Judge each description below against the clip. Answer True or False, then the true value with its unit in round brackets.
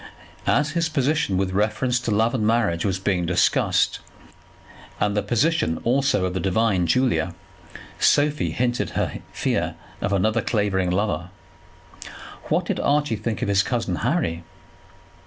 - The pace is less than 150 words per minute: True (140 wpm)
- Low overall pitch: True (105 Hz)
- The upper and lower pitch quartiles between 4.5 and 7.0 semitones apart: True (5.1 semitones)